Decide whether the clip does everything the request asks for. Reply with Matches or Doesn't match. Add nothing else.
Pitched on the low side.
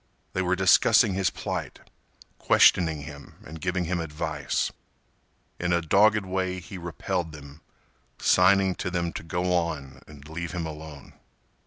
Matches